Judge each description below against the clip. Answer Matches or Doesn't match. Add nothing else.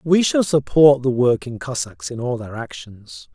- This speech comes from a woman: Doesn't match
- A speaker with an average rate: Matches